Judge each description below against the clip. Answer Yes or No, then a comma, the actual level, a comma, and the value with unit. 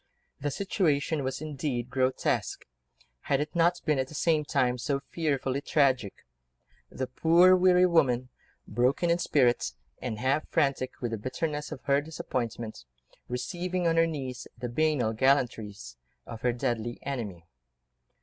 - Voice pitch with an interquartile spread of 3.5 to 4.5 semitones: Yes, average, 4.1 semitones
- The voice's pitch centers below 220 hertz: Yes, low, 135 Hz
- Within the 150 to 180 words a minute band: No, average, 140 wpm